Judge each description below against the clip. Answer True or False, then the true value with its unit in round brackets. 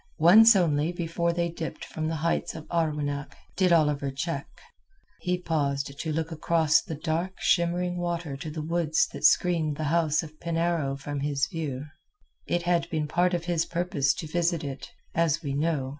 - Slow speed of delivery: False (175 wpm)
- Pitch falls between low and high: True (160 Hz)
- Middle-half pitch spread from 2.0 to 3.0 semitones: True (2.4 semitones)